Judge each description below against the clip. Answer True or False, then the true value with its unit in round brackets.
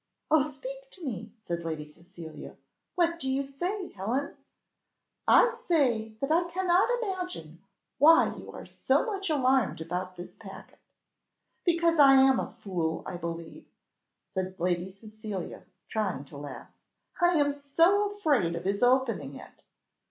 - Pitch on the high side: True (255 Hz)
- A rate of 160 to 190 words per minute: False (145 wpm)